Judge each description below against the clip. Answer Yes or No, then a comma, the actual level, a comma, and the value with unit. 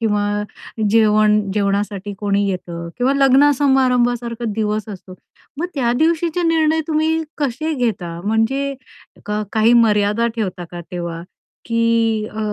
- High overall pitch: Yes, high, 225 Hz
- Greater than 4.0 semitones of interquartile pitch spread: Yes, average, 4.6 semitones